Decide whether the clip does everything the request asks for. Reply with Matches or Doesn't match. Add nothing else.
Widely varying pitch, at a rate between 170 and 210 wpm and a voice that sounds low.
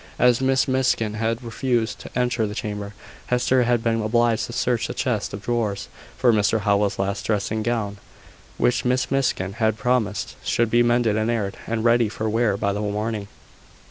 Doesn't match